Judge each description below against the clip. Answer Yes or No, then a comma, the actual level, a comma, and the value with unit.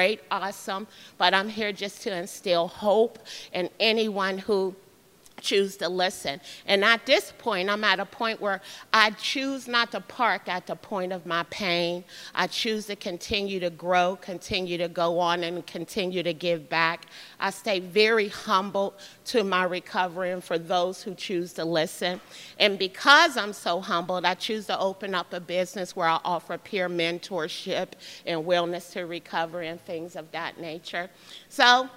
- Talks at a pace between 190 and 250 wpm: No, average, 170 wpm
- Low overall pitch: No, medium, 185 Hz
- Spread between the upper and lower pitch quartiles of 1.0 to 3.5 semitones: Yes, average, 2.8 semitones